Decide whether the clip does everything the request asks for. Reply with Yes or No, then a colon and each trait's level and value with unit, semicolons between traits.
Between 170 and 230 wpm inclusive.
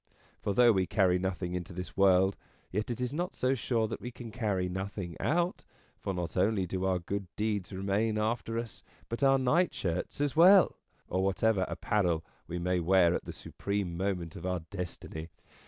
Yes: average, 185 wpm